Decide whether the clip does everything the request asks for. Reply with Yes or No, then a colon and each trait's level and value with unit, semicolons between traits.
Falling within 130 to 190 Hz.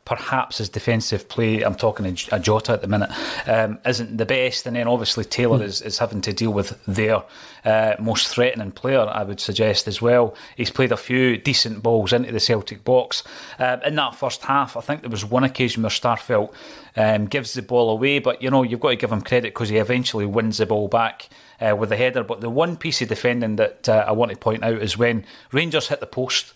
No: low, 115 Hz